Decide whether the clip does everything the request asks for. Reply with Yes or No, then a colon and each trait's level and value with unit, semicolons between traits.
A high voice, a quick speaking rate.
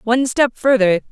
No: high, 240 Hz; average, 160 wpm